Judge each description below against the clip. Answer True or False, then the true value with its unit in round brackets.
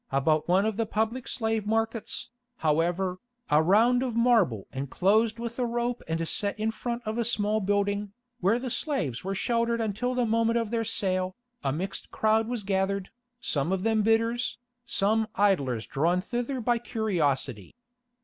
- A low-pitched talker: False (215 Hz)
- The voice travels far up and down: False (4.0 semitones)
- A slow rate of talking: False (165 wpm)